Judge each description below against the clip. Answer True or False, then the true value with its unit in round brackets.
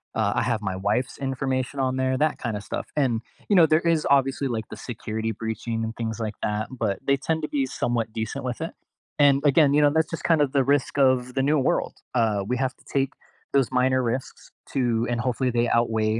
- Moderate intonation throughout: True (3.5 semitones)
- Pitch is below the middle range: True (130 Hz)